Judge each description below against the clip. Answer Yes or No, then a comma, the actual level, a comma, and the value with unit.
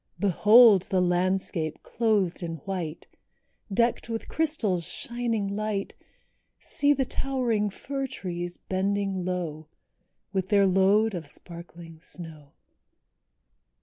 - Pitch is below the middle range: No, high, 195 Hz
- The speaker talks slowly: Yes, slow, 105 wpm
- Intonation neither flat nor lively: Yes, average, 4.0 semitones